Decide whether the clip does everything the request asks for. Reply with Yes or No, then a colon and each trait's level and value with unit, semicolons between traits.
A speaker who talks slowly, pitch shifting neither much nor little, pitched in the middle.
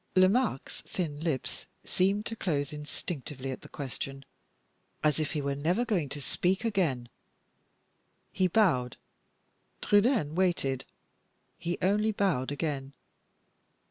No: slow, 115 wpm; wide, 5.7 semitones; medium, 160 Hz